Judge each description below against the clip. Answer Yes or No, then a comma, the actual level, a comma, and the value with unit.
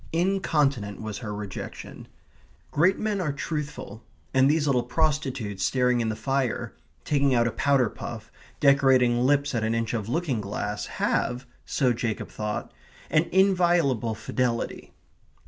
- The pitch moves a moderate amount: Yes, average, 4.8 semitones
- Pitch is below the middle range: Yes, low, 130 Hz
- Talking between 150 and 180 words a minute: No, average, 140 wpm